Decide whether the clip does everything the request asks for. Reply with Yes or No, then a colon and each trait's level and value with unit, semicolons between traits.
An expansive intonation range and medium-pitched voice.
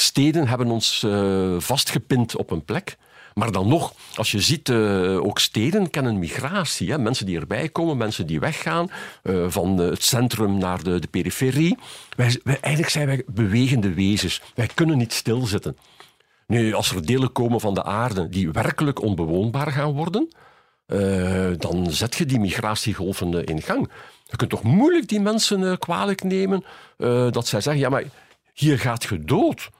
No: wide, 7.0 semitones; low, 120 Hz